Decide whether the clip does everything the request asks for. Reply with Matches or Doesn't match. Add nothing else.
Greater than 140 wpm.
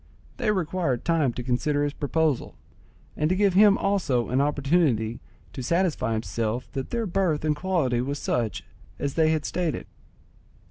Matches